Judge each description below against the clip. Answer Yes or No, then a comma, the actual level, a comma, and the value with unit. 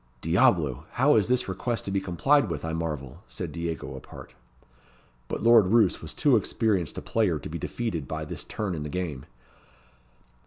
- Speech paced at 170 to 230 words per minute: Yes, average, 180 wpm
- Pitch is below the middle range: Yes, very low, 90 Hz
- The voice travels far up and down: Yes, wide, 6.0 semitones